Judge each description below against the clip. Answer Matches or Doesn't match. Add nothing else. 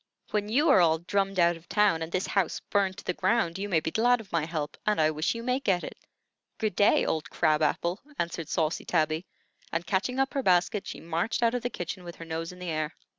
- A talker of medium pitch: Matches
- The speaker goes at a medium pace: Doesn't match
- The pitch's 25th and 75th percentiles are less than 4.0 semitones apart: Doesn't match